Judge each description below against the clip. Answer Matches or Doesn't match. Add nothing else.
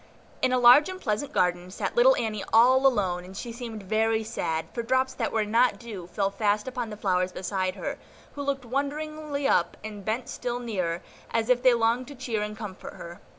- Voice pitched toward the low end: Doesn't match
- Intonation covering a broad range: Doesn't match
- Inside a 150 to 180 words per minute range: Doesn't match